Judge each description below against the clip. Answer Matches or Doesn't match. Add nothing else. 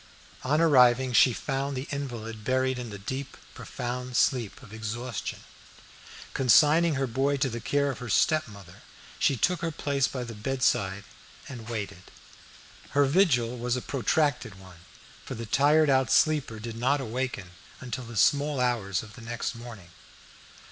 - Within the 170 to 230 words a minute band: Doesn't match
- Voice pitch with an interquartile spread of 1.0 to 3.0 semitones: Doesn't match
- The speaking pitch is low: Matches